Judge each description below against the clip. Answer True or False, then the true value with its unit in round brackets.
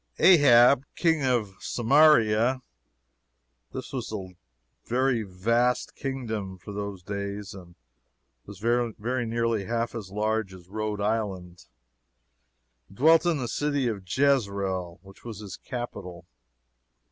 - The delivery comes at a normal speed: False (115 wpm)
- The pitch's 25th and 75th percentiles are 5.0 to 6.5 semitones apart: False (4.1 semitones)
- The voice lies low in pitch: True (110 Hz)